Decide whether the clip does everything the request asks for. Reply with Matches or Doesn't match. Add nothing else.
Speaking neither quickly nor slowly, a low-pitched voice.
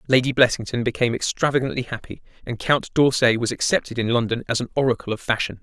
Matches